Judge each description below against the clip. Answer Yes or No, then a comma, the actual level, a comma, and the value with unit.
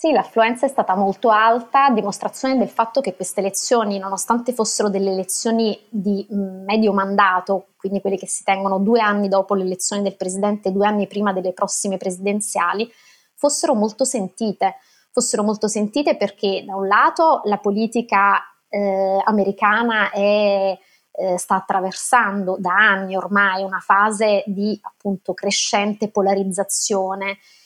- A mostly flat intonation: Yes, narrow, 1.9 semitones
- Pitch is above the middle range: Yes, high, 200 Hz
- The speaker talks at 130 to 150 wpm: Yes, average, 140 wpm